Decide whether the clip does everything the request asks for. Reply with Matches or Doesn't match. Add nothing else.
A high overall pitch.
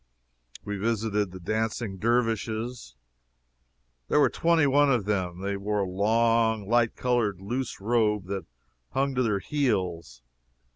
Doesn't match